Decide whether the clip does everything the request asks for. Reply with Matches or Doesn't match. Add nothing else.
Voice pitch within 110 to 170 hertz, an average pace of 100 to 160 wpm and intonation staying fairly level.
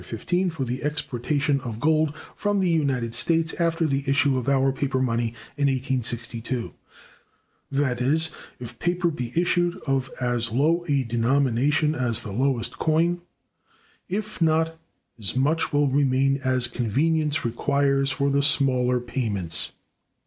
Doesn't match